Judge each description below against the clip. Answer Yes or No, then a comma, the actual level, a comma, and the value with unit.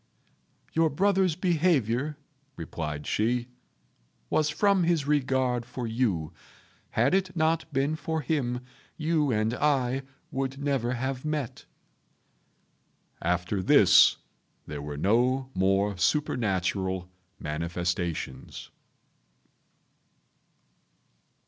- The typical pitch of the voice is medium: No, low, 130 Hz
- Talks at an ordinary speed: No, slow, 90 wpm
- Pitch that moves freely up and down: Yes, wide, 7.5 semitones